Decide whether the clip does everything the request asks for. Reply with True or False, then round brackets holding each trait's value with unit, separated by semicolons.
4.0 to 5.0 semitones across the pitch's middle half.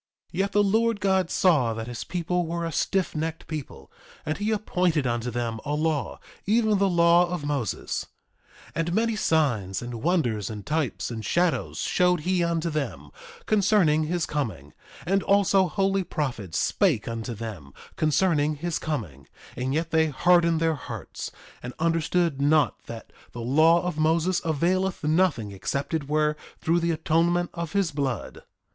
True (4.7 semitones)